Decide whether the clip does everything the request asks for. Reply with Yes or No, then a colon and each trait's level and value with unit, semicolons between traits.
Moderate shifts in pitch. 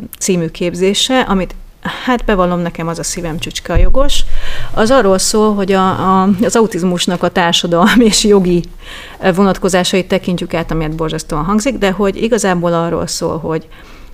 Yes: average, 3.0 semitones